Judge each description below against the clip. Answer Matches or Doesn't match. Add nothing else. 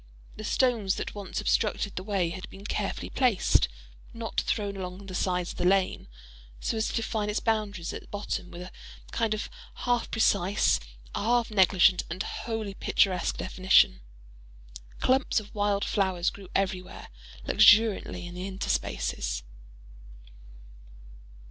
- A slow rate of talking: Matches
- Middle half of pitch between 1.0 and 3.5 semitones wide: Matches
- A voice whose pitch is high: Matches